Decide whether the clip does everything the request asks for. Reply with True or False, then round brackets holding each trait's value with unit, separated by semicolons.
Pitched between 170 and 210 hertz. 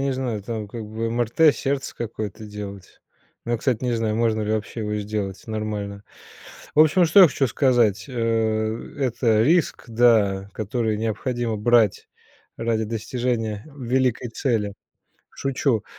False (115 Hz)